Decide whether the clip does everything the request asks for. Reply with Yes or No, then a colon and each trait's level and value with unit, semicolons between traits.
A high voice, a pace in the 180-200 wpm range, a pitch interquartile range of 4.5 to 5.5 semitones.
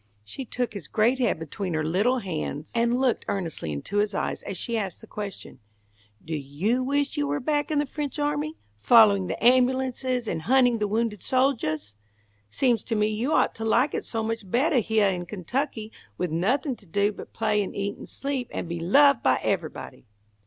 Yes: high, 225 Hz; average, 195 wpm; average, 5.1 semitones